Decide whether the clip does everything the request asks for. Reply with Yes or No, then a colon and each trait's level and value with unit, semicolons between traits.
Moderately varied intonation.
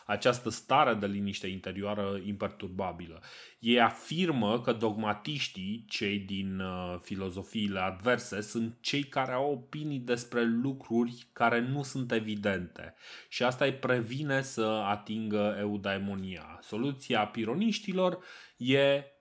Yes: average, 4.8 semitones